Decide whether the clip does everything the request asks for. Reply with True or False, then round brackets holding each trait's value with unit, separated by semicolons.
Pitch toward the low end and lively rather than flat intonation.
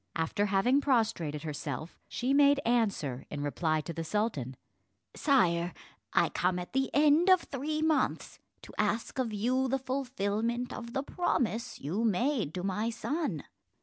False (225 Hz; 7.3 semitones)